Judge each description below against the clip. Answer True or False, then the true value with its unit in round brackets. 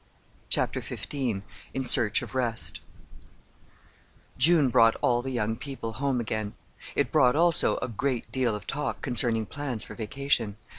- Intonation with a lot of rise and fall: False (3.4 semitones)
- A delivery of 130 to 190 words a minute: True (145 wpm)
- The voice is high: False (125 Hz)